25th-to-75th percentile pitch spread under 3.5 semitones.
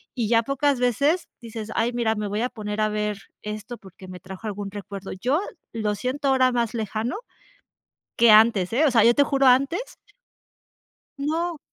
No: average, 4.0 semitones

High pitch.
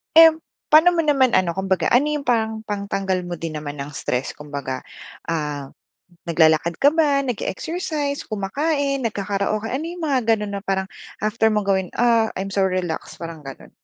Yes: high, 205 Hz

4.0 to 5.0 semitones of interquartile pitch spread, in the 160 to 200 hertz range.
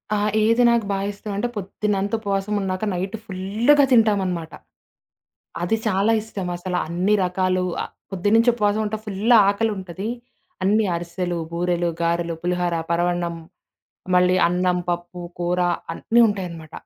No: average, 3.1 semitones; high, 190 Hz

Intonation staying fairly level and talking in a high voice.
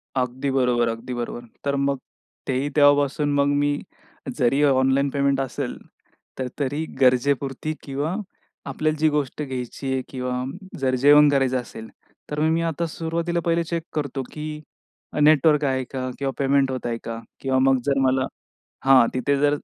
No: narrow, 2.1 semitones; medium, 140 Hz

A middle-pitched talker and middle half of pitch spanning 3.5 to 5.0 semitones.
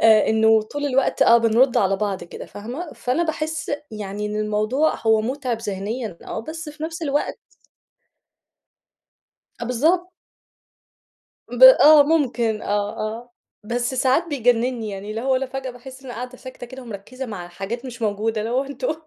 No: high, 245 Hz; average, 4.1 semitones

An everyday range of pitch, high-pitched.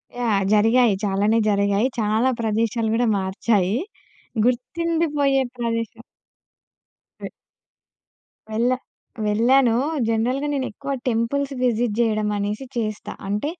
Yes: average, 3.1 semitones; high, 230 Hz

